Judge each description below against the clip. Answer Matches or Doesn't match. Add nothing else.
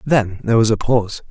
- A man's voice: Matches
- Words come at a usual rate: Doesn't match